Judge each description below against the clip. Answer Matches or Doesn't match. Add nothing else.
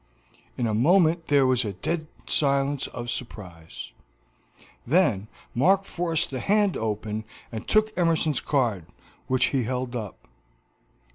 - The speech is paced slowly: Matches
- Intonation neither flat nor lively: Doesn't match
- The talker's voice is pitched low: Matches